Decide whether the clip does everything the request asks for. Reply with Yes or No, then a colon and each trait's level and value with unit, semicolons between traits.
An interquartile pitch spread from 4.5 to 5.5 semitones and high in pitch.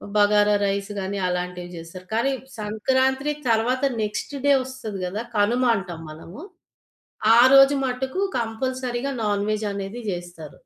Yes: average, 4.8 semitones; high, 210 Hz